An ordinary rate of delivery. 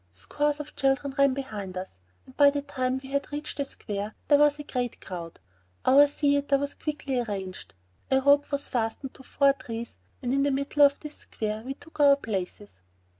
Yes: average, 195 wpm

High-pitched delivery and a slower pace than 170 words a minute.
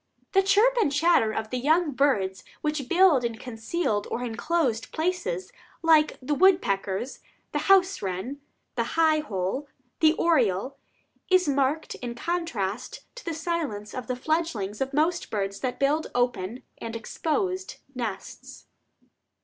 Yes: very high, 275 Hz; average, 140 wpm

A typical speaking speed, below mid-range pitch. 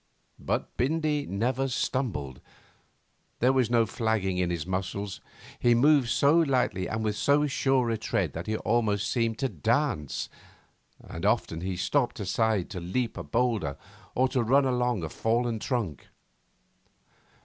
Yes: average, 150 wpm; low, 115 Hz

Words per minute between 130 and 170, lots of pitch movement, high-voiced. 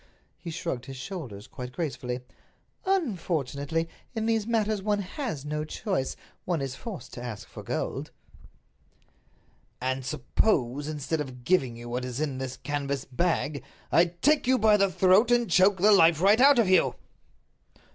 No: average, 155 wpm; wide, 7.5 semitones; medium, 165 Hz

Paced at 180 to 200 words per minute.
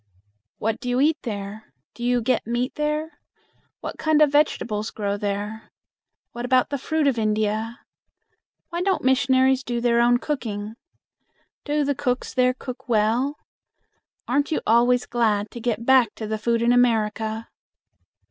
No: average, 155 wpm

